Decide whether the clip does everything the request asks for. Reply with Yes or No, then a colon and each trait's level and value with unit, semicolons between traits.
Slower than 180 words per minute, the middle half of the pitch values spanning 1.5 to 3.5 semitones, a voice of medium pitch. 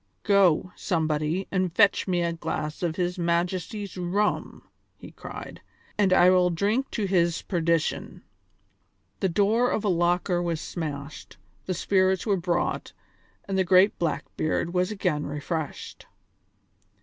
Yes: slow, 135 wpm; narrow, 2.4 semitones; medium, 180 Hz